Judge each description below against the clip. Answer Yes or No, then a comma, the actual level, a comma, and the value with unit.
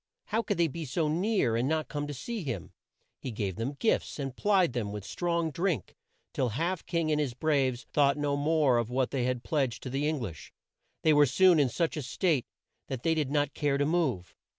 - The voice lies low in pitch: No, medium, 145 Hz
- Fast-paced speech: Yes, fast, 220 wpm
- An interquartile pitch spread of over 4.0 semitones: Yes, average, 4.4 semitones